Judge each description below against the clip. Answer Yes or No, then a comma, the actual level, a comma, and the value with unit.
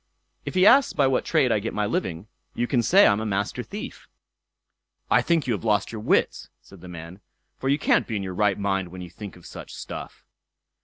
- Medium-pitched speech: No, low, 105 Hz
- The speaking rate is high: Yes, fast, 220 wpm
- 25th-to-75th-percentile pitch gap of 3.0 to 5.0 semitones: No, wide, 5.6 semitones